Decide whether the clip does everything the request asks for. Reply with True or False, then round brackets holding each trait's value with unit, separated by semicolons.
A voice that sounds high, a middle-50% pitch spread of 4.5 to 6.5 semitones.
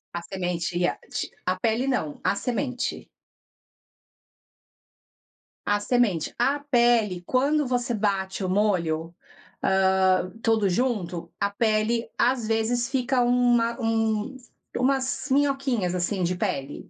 True (220 Hz; 4.8 semitones)